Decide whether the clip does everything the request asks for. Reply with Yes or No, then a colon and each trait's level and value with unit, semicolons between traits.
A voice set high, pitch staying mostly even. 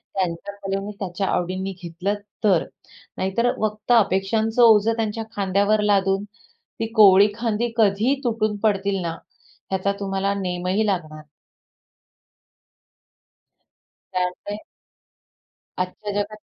Yes: high, 200 Hz; narrow, 2.3 semitones